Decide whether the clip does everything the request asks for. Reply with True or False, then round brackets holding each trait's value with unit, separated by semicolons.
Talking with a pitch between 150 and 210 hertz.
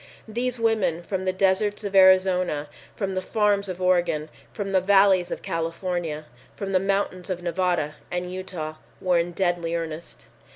True (185 Hz)